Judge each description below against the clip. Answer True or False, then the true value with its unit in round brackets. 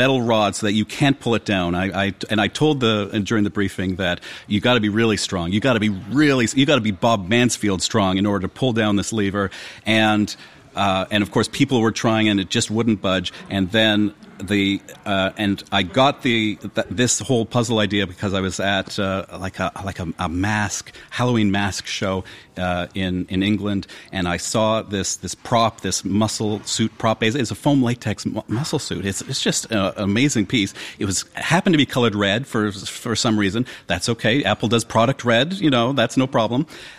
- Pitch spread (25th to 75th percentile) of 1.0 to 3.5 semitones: True (3.1 semitones)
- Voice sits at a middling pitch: False (105 Hz)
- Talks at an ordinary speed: False (220 wpm)